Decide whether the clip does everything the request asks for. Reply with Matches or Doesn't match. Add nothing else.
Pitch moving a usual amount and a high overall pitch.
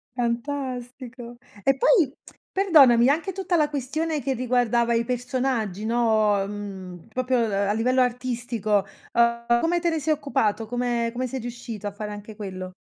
Matches